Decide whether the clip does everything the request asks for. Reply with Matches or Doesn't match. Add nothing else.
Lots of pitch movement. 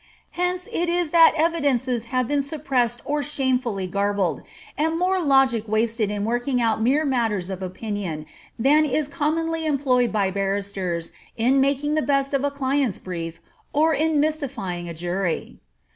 Matches